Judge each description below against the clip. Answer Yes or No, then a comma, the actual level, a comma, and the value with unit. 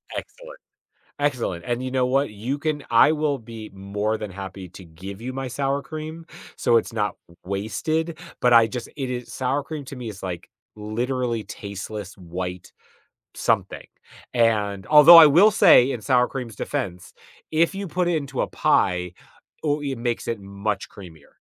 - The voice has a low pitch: Yes, low, 120 Hz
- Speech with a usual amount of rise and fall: No, wide, 6.1 semitones